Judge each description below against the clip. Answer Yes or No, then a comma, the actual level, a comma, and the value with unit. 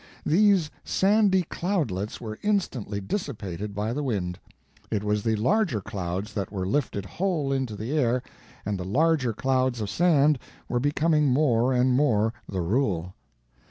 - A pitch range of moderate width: No, wide, 6.6 semitones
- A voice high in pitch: No, low, 125 Hz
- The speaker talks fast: No, average, 150 wpm